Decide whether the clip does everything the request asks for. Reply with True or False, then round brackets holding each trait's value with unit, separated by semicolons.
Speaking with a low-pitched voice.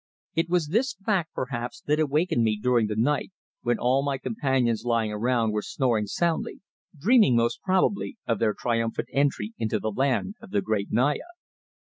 True (125 Hz)